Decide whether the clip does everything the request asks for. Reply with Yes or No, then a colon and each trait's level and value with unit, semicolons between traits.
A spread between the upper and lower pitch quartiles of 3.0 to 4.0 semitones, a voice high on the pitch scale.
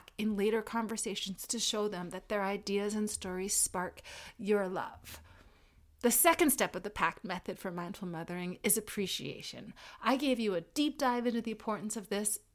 Yes: average, 3.5 semitones; high, 205 Hz